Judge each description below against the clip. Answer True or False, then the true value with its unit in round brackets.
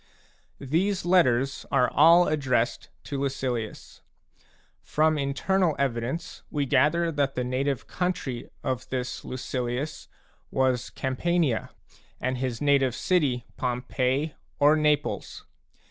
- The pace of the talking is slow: True (105 wpm)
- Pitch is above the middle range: False (140 Hz)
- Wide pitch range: False (3.5 semitones)